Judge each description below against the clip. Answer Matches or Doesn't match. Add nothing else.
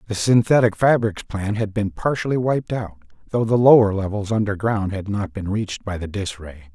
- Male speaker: Matches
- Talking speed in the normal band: Matches